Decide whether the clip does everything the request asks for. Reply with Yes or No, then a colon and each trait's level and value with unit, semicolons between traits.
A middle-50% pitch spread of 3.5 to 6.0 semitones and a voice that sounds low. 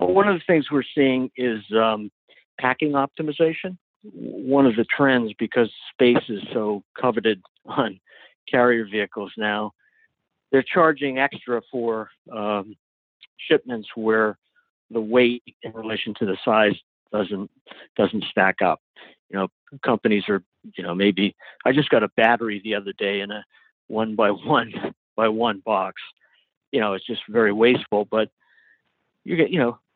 Yes: average, 4.5 semitones; low, 115 Hz